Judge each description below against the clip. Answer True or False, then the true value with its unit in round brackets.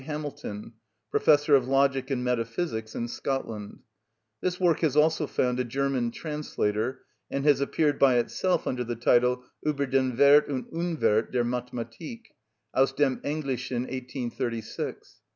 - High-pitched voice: False (130 Hz)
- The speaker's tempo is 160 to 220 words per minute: False (135 wpm)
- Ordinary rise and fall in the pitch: True (3.4 semitones)